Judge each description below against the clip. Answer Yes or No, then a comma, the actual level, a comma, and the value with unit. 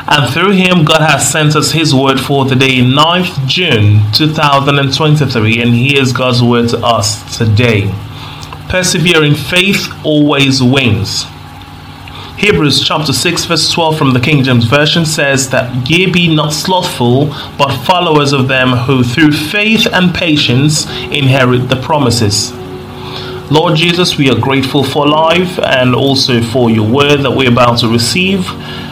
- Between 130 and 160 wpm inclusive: Yes, average, 145 wpm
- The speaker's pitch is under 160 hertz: Yes, medium, 140 Hz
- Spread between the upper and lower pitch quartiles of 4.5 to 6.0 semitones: No, average, 4.0 semitones